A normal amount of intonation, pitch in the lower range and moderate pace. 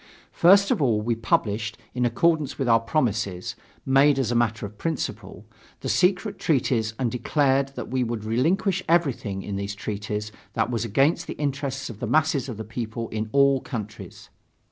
Yes: average, 4.4 semitones; low, 120 Hz; average, 175 wpm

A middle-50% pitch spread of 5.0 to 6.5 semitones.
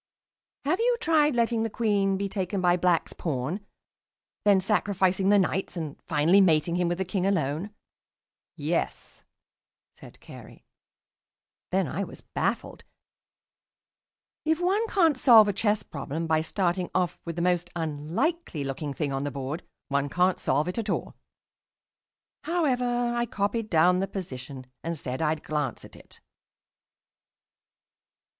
Yes: wide, 5.4 semitones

